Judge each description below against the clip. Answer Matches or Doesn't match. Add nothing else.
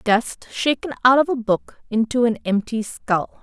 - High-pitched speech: Matches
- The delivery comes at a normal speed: Matches